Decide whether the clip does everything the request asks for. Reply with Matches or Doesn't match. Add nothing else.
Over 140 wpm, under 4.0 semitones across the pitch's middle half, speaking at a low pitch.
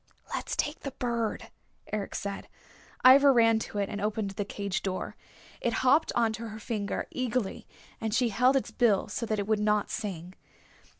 Doesn't match